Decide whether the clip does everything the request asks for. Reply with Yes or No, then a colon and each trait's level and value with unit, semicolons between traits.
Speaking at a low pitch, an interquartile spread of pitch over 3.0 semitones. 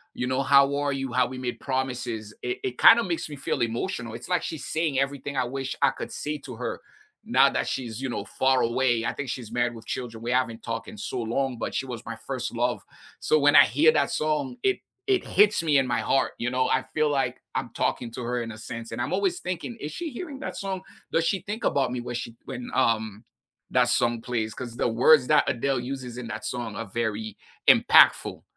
Yes: low, 130 Hz; average, 3.6 semitones